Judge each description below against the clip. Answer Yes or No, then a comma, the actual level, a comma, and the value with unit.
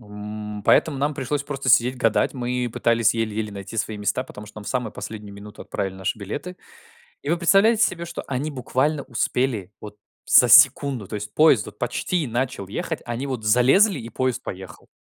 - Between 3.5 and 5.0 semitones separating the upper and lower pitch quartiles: Yes, average, 4.7 semitones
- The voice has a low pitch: Yes, low, 120 Hz